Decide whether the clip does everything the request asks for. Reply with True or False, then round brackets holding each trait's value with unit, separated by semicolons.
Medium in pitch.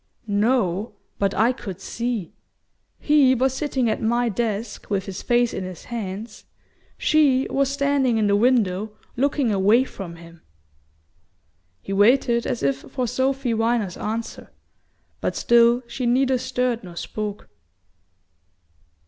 False (235 Hz)